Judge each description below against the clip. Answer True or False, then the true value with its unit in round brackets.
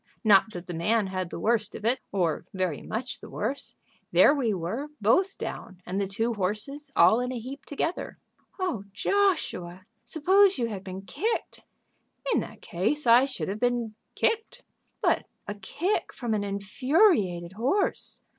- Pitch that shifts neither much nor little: False (6.6 semitones)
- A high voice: True (225 Hz)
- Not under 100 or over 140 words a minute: False (165 wpm)